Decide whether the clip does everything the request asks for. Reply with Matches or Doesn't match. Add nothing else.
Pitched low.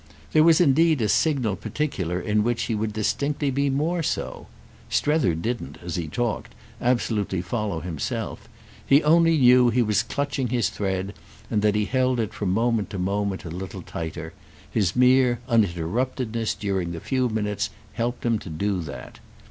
Matches